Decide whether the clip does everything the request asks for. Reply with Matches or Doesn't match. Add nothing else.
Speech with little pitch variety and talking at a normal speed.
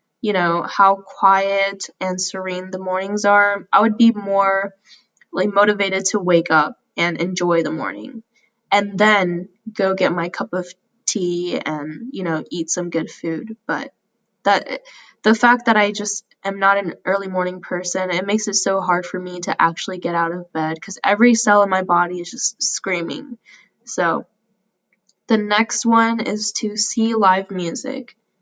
Doesn't match